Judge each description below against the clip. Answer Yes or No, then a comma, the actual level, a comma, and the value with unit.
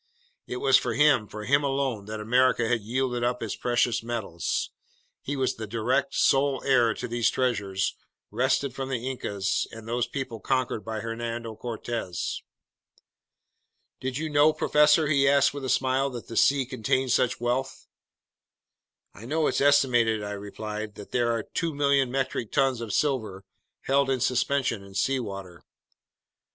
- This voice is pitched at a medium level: No, low, 125 Hz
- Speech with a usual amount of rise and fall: Yes, average, 3.3 semitones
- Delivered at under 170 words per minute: Yes, average, 160 wpm